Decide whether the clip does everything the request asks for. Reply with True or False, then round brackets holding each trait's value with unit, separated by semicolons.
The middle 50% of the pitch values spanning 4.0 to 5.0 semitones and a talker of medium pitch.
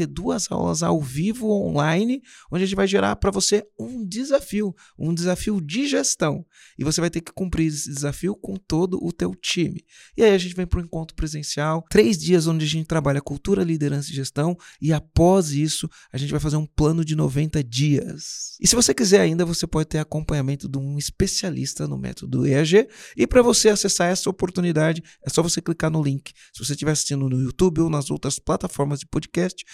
True (4.6 semitones; 165 Hz)